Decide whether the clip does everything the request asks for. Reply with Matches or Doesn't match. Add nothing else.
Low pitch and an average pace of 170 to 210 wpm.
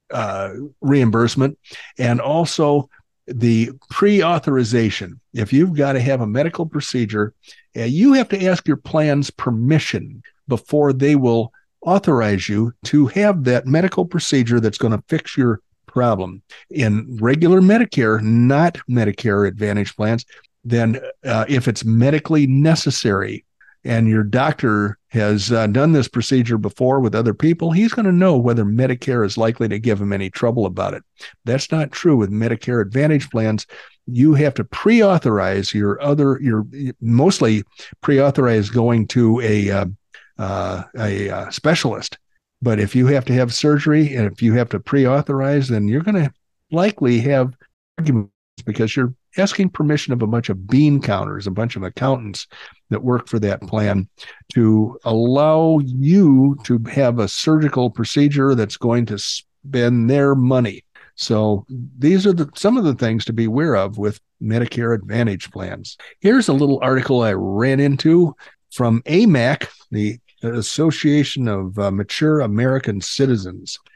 Doesn't match